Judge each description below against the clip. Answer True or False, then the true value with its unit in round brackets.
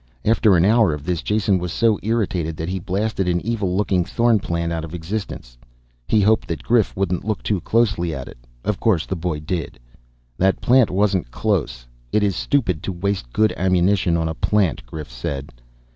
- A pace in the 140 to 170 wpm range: False (190 wpm)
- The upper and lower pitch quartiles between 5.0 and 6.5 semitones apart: False (4.3 semitones)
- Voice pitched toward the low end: True (95 Hz)